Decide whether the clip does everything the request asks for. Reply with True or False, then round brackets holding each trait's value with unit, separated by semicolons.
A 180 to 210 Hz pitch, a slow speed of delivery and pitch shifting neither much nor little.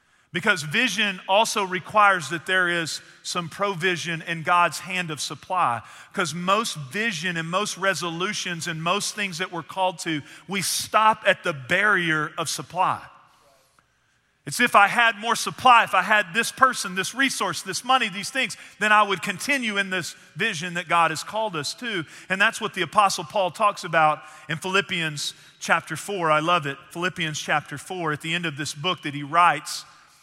False (185 Hz; 180 wpm; 3.6 semitones)